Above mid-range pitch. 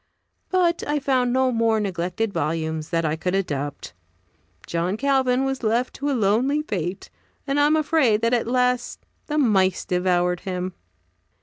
Yes: high, 225 Hz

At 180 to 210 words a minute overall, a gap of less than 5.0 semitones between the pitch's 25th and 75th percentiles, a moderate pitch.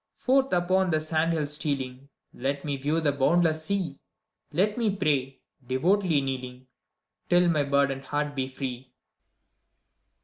No: slow, 135 wpm; average, 4.5 semitones; medium, 150 Hz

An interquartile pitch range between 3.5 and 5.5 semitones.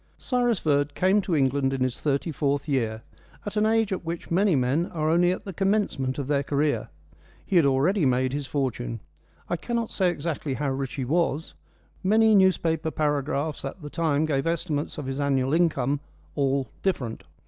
Yes: average, 4.4 semitones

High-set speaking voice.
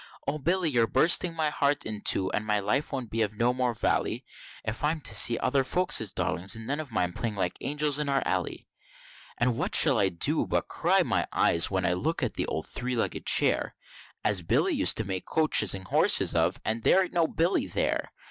No: low, 120 Hz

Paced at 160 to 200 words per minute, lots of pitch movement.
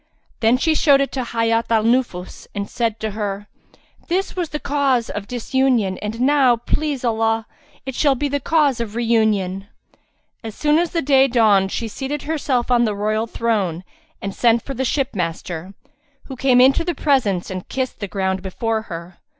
No: average, 180 wpm; average, 4.6 semitones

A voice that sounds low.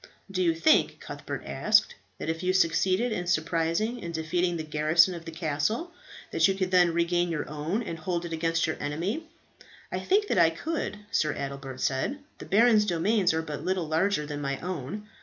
No: medium, 170 Hz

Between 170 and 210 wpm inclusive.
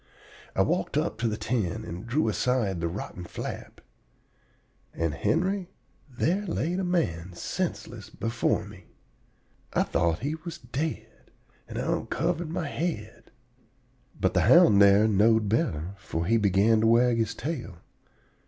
No: average, 145 wpm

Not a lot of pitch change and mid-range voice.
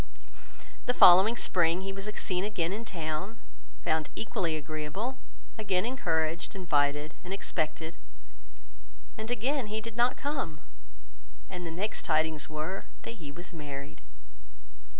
No: wide, 5.4 semitones; medium, 180 Hz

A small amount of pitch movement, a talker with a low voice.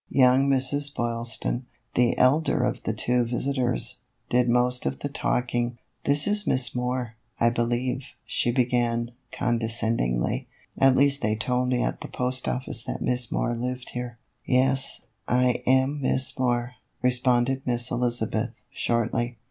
Yes: narrow, 1.5 semitones; low, 125 Hz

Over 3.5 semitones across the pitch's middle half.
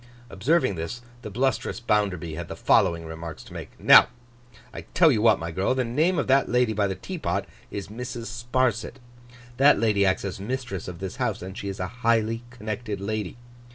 Yes: average, 4.5 semitones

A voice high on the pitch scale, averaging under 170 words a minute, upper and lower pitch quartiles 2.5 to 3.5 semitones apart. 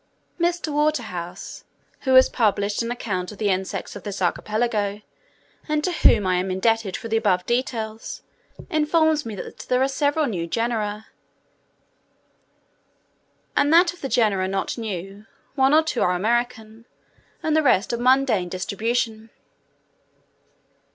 No: high, 225 Hz; average, 140 wpm; average, 5.0 semitones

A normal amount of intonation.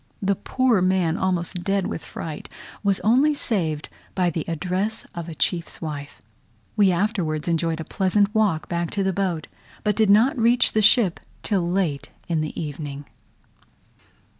Yes: average, 4.2 semitones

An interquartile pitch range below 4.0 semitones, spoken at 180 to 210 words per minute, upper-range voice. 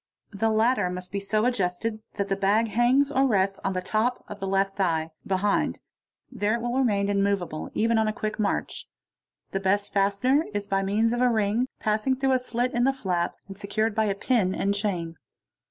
Yes: average, 3.0 semitones; average, 200 wpm; high, 205 Hz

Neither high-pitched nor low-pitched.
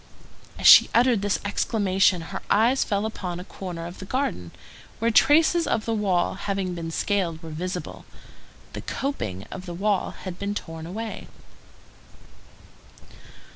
No: high, 195 Hz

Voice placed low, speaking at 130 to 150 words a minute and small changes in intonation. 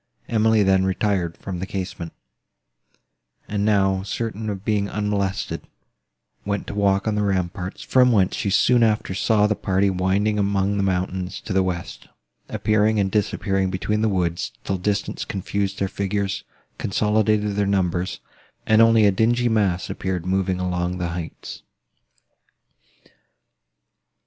Yes: low, 100 Hz; average, 140 wpm; narrow, 2.1 semitones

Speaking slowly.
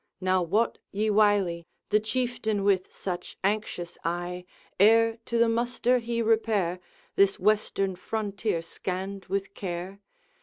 Yes: slow, 125 wpm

